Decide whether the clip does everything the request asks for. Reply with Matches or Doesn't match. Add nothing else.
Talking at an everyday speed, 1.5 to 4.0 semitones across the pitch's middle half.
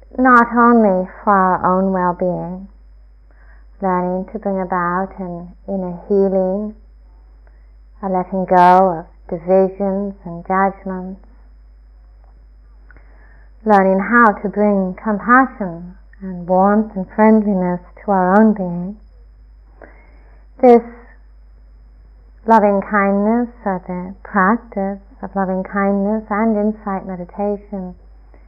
Doesn't match